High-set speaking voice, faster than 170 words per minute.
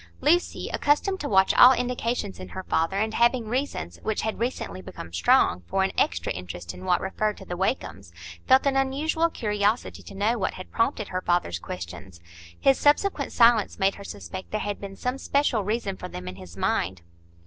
Yes: high, 200 Hz; average, 190 wpm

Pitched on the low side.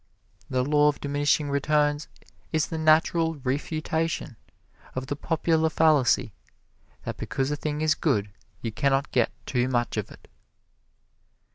No: medium, 145 Hz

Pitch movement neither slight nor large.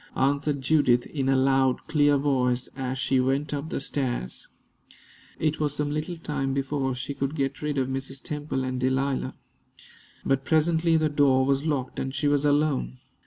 No: narrow, 1.9 semitones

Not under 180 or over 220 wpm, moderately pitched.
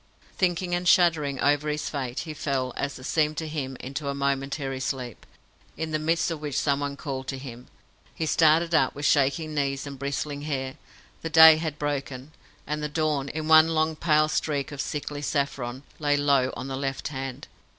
Yes: average, 190 wpm; medium, 145 Hz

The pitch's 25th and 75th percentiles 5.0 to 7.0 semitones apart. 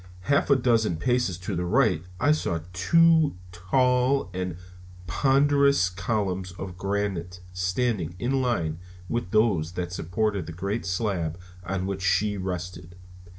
Yes: wide, 5.4 semitones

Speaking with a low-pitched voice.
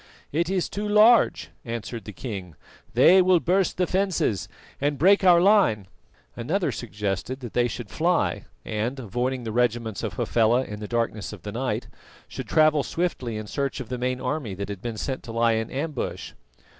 Yes: low, 125 Hz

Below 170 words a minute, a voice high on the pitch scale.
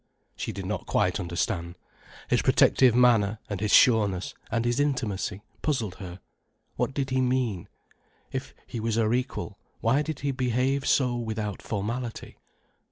No: average, 150 wpm; low, 115 Hz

